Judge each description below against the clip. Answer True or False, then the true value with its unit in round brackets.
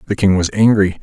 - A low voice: True (100 Hz)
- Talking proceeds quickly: True (235 wpm)